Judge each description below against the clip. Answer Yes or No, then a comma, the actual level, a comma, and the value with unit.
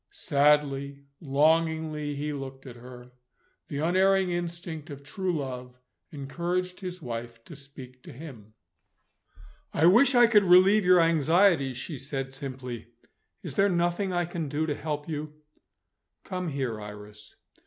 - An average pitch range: Yes, average, 4.6 semitones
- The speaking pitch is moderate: Yes, medium, 150 Hz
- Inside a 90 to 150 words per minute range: Yes, average, 140 wpm